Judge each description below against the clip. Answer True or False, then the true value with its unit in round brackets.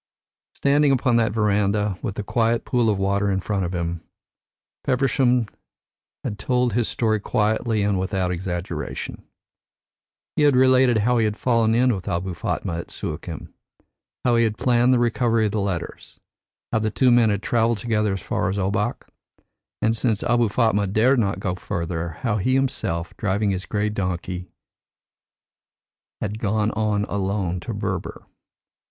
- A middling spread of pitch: True (3.5 semitones)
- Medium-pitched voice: False (105 Hz)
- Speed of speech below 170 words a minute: True (160 wpm)